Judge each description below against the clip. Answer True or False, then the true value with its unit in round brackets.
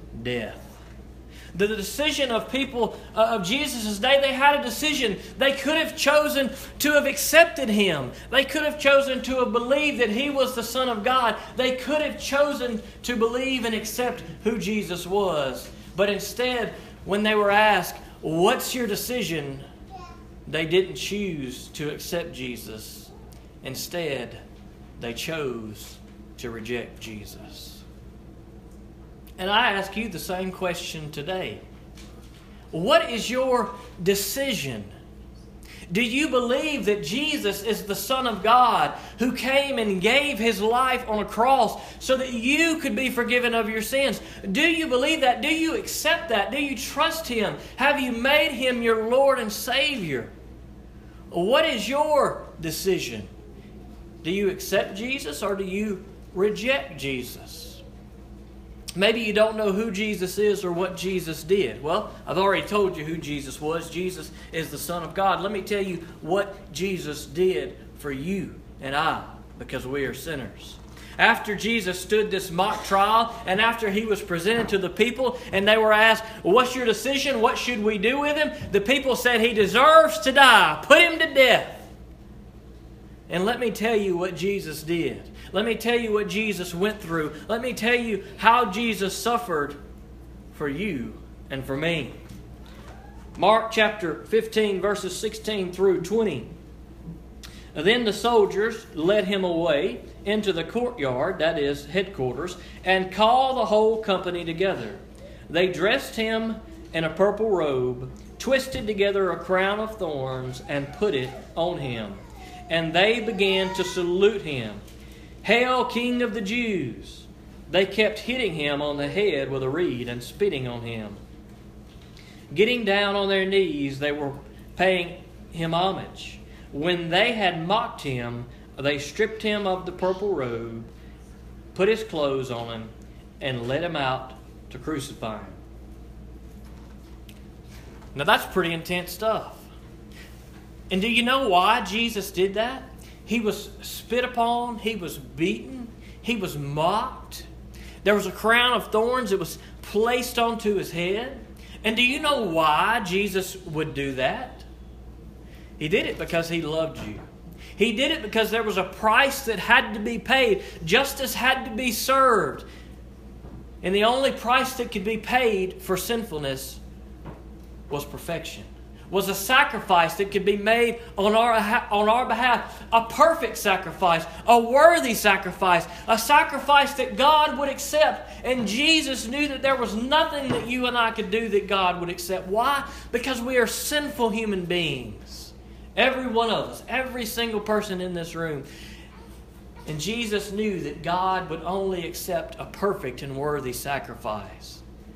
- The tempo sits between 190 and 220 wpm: False (155 wpm)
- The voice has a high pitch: True (200 Hz)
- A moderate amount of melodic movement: False (6.7 semitones)